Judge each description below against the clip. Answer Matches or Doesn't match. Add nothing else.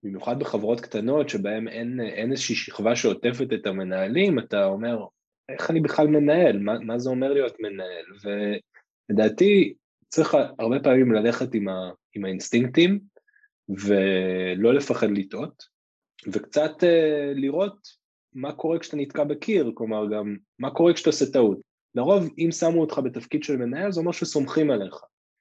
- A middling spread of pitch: Doesn't match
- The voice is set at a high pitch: Doesn't match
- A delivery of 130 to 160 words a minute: Matches